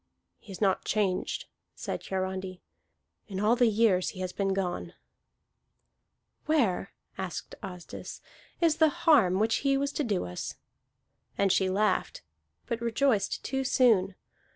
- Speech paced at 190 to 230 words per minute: No, slow, 135 wpm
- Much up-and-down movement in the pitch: No, average, 4.8 semitones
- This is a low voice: No, high, 200 Hz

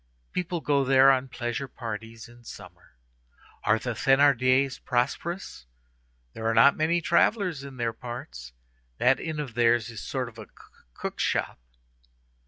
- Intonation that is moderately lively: Yes, average, 3.4 semitones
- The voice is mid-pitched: No, low, 125 Hz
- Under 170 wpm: Yes, average, 150 wpm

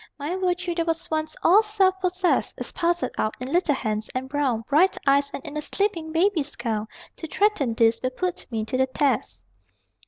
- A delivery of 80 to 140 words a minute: No, average, 195 wpm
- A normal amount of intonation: No, wide, 5.7 semitones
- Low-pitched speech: No, very high, 305 Hz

